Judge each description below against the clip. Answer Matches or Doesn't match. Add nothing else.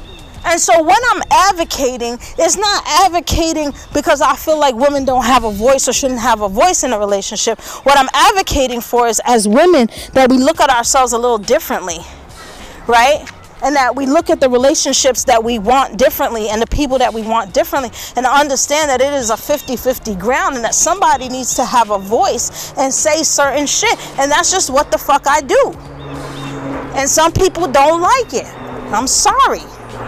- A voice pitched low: Doesn't match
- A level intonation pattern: Doesn't match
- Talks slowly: Doesn't match